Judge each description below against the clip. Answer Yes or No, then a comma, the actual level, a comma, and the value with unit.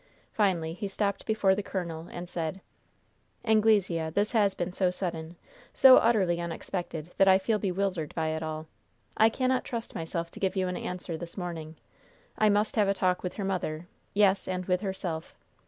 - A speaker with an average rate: Yes, average, 180 wpm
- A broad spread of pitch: No, average, 3.2 semitones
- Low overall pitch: No, medium, 185 Hz